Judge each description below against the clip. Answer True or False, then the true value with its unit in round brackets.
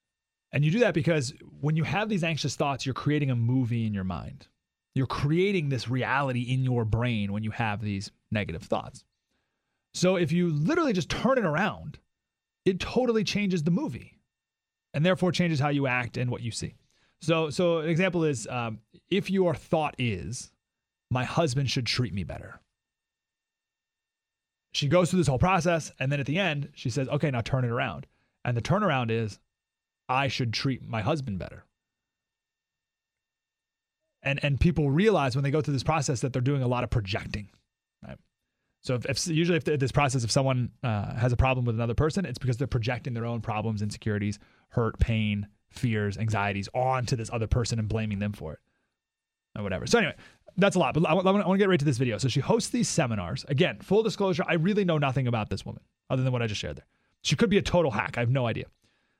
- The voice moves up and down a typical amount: False (6.1 semitones)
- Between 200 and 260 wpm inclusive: True (205 wpm)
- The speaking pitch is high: False (135 Hz)